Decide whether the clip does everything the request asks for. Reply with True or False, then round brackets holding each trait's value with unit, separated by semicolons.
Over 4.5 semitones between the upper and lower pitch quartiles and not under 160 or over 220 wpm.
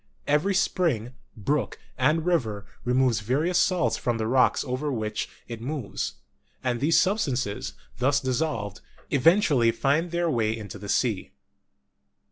False (5.6 semitones; 135 wpm)